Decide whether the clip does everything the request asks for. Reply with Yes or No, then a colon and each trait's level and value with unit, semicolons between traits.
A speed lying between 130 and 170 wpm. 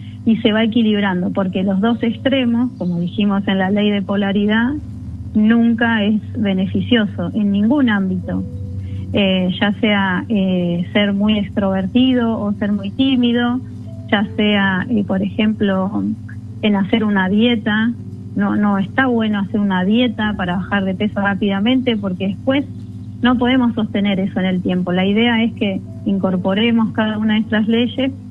Yes: average, 155 wpm